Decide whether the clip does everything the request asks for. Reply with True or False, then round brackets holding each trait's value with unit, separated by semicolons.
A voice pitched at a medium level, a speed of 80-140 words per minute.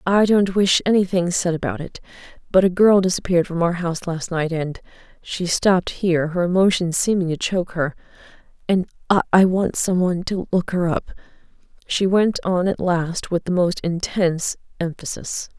False (180 Hz; 165 wpm)